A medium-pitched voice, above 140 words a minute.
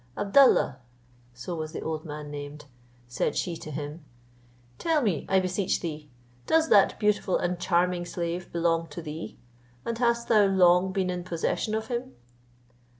Yes: medium, 175 Hz; average, 155 wpm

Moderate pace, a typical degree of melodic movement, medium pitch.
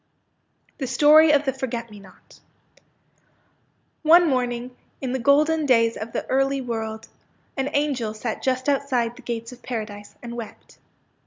No: average, 150 wpm; average, 3.3 semitones; very high, 250 Hz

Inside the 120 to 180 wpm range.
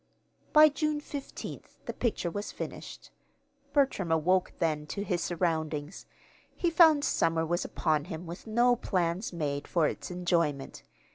Yes: average, 140 wpm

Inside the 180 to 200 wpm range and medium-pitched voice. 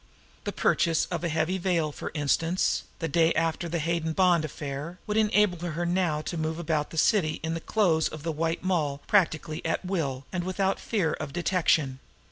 Yes: average, 190 wpm; medium, 165 Hz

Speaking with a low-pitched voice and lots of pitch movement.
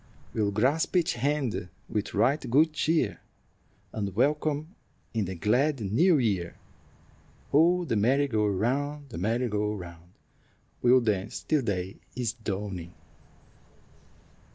Yes: low, 115 Hz; wide, 6.1 semitones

